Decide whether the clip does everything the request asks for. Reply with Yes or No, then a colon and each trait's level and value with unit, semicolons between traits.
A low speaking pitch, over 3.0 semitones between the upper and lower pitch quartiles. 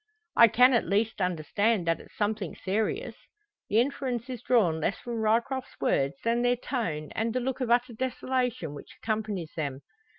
No: high, 225 Hz; average, 4.9 semitones